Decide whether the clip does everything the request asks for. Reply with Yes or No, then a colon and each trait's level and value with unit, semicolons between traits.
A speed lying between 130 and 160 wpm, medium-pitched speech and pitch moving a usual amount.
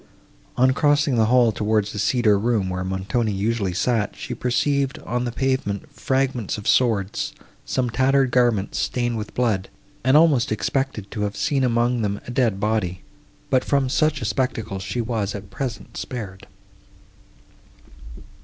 No: average, 155 wpm; low, 120 Hz; average, 4.0 semitones